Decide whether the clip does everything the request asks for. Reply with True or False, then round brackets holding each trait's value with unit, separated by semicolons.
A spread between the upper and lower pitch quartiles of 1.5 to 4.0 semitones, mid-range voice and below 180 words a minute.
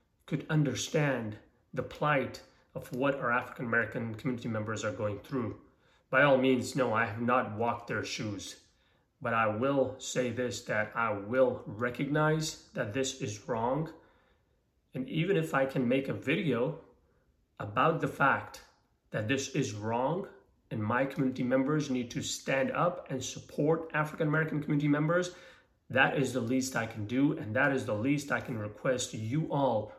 False (3.6 semitones; 130 Hz; 165 wpm)